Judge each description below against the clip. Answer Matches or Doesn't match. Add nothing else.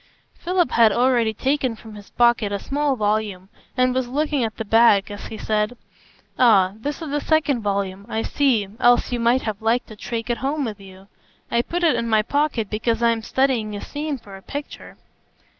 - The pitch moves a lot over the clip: Doesn't match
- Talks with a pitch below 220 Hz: Doesn't match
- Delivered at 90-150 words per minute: Doesn't match